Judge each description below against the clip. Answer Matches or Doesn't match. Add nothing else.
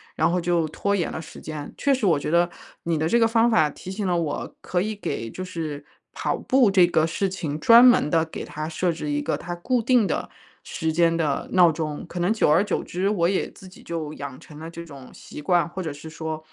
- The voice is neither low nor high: Matches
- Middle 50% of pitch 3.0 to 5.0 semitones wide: Matches